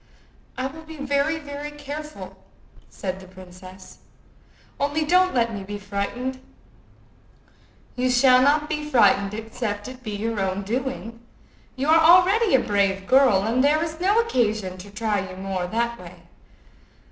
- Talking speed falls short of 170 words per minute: Yes, average, 150 wpm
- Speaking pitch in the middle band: No, very high, 250 Hz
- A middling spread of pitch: No, wide, 6.5 semitones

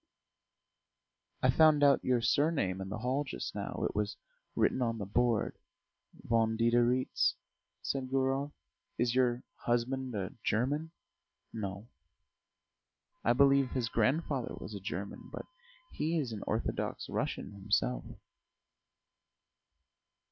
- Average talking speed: No, slow, 120 wpm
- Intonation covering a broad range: No, average, 4.0 semitones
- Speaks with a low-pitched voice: Yes, low, 120 Hz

